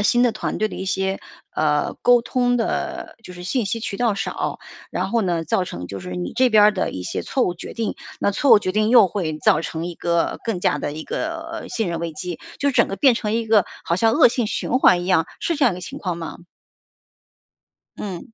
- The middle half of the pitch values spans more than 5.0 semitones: Yes, wide, 5.4 semitones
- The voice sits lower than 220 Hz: Yes, high, 195 Hz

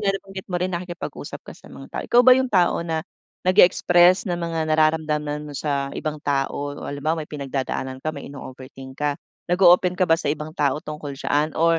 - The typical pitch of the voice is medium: Yes, medium, 155 Hz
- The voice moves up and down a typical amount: Yes, average, 3.5 semitones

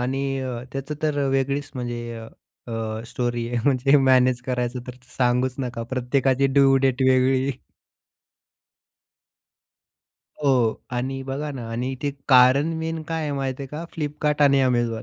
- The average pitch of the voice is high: No, low, 130 Hz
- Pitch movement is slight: Yes, narrow, 2.0 semitones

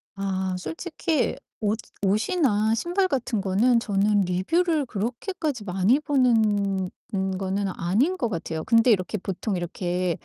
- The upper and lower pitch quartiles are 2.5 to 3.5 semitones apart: No, average, 5.1 semitones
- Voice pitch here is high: Yes, high, 210 Hz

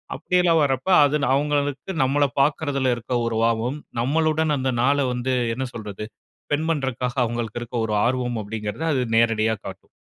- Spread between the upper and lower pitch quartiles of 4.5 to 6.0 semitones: No, average, 3.8 semitones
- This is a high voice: No, low, 130 Hz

